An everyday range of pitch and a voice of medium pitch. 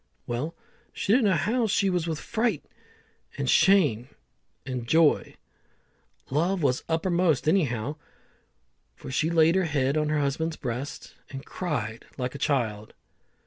Yes: average, 5.0 semitones; medium, 155 Hz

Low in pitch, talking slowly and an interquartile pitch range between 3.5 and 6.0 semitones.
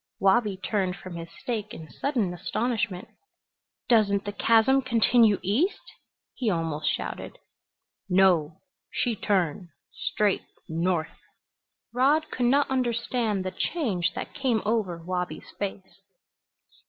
No: high, 205 Hz; slow, 115 wpm; average, 4.8 semitones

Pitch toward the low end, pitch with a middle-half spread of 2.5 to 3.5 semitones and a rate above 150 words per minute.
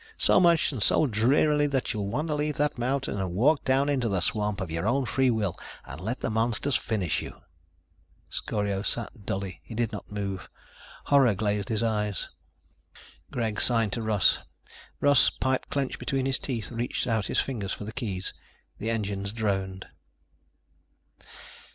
No: low, 110 Hz; average, 4.7 semitones; average, 165 wpm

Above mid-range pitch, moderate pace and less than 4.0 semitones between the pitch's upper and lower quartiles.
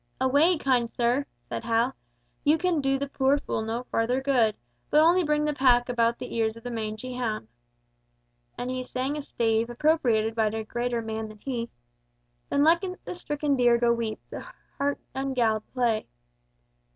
Yes: high, 245 Hz; average, 175 wpm; average, 3.6 semitones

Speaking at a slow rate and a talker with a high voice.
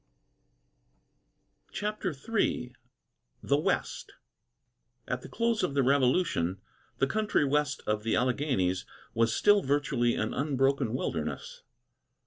No: slow, 110 wpm; low, 135 Hz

